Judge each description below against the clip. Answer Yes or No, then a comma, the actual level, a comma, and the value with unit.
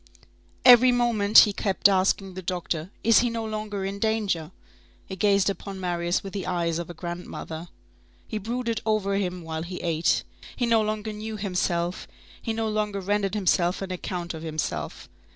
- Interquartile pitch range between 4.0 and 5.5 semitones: No, average, 3.5 semitones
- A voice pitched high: Yes, high, 195 Hz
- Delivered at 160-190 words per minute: Yes, average, 170 wpm